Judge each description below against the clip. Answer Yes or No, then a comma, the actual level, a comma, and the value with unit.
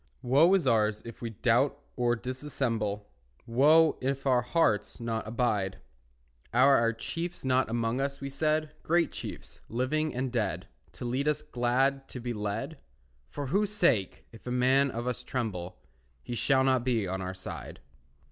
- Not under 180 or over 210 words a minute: No, average, 165 wpm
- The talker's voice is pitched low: Yes, low, 125 Hz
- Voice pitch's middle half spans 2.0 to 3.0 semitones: No, average, 3.4 semitones